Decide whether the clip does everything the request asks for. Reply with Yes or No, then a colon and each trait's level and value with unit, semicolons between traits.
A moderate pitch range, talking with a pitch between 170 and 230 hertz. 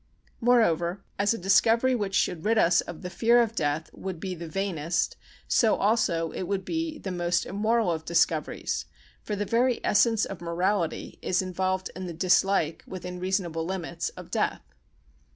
Yes: average, 3.9 semitones; medium, 185 Hz